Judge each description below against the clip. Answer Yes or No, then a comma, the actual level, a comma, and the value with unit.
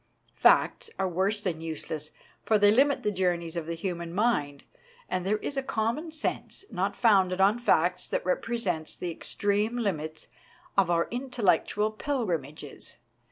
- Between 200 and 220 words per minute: No, average, 155 wpm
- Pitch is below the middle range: No, high, 195 Hz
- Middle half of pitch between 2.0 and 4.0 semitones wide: No, average, 4.7 semitones